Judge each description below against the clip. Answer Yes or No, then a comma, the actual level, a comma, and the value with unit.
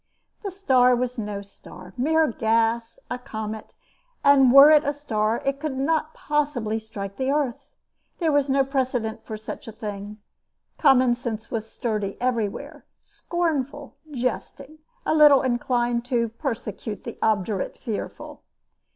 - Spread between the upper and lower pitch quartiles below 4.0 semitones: No, average, 4.3 semitones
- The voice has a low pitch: No, high, 245 Hz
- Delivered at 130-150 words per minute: Yes, average, 140 wpm